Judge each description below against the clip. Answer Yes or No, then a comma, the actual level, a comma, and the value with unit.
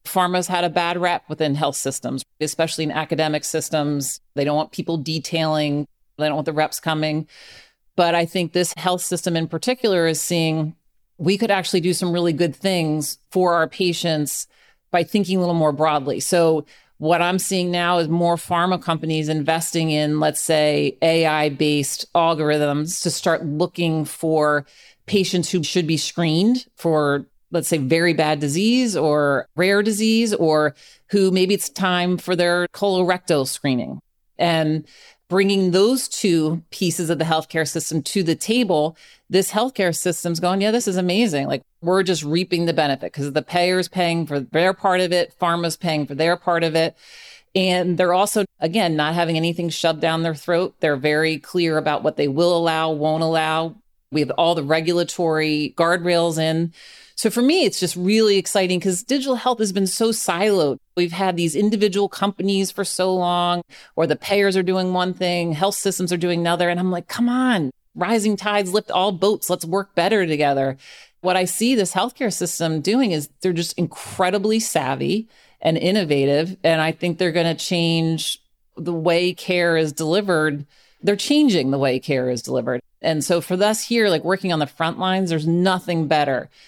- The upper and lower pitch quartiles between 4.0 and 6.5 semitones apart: No, average, 2.9 semitones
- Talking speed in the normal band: Yes, average, 180 wpm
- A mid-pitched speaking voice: Yes, medium, 170 Hz